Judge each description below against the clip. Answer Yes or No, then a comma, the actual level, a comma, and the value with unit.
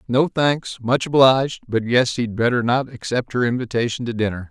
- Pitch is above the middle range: No, low, 120 Hz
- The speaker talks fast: No, average, 185 wpm